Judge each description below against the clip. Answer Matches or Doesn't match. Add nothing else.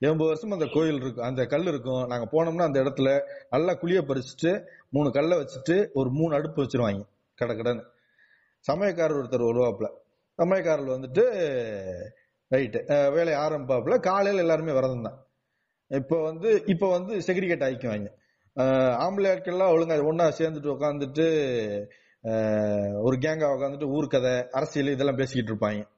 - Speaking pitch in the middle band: Matches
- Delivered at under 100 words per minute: Doesn't match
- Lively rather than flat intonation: Doesn't match